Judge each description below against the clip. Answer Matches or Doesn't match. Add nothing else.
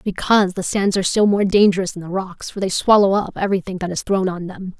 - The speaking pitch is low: Doesn't match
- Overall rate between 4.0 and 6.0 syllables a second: Doesn't match